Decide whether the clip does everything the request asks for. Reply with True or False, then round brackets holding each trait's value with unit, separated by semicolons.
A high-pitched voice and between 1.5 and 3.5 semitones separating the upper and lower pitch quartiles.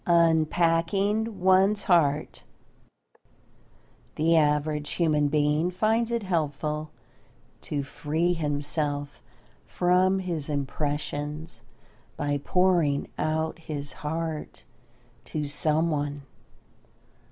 False (155 Hz; 3.2 semitones)